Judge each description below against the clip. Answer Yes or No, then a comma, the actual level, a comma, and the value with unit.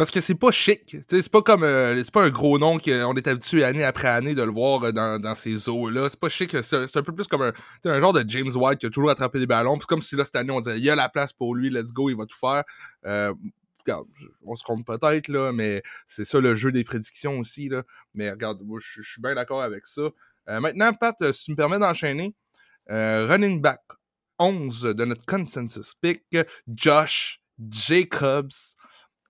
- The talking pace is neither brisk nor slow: No, fast, 225 wpm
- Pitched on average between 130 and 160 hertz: Yes, low, 135 Hz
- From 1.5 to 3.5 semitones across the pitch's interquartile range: No, average, 5.3 semitones